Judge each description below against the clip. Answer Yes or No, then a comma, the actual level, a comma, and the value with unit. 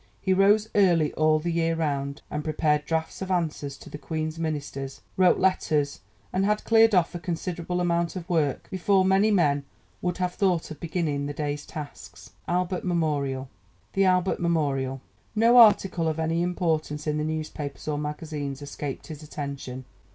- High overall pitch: No, medium, 160 Hz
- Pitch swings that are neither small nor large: Yes, average, 3.5 semitones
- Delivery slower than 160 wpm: No, average, 165 wpm